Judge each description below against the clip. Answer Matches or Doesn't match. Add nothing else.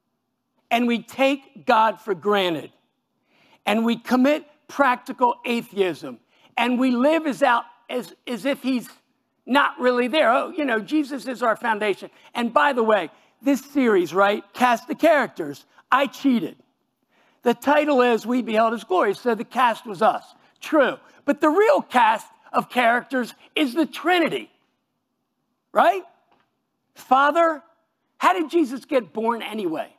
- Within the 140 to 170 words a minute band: Matches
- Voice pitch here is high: Matches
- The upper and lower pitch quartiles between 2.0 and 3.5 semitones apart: Doesn't match